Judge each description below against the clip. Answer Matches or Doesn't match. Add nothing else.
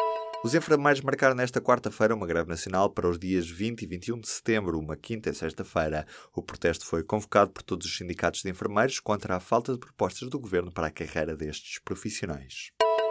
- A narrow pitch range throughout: Doesn't match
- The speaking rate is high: Matches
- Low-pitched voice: Matches